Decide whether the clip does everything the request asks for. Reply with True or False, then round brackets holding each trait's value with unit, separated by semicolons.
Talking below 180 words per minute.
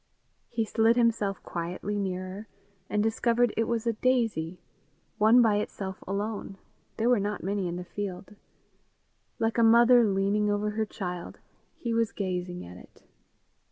True (150 wpm)